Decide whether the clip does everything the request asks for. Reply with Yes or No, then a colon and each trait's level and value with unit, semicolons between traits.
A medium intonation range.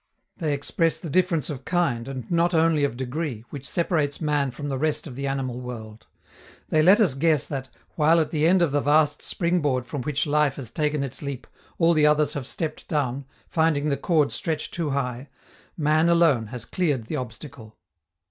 Yes: average, 3.3 semitones